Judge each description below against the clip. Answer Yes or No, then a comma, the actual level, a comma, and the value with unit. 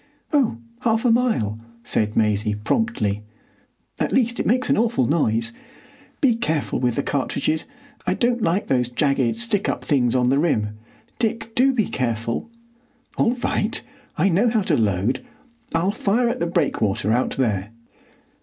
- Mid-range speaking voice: Yes, medium, 155 Hz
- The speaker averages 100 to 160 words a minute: Yes, average, 155 wpm